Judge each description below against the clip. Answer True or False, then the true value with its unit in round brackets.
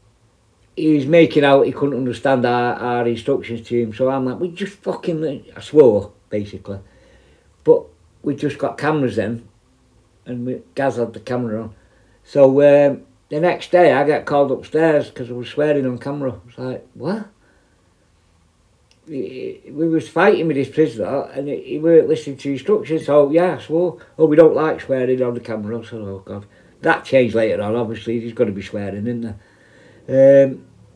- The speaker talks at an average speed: True (180 wpm)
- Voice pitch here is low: True (125 Hz)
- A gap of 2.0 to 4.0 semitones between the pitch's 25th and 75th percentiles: False (4.6 semitones)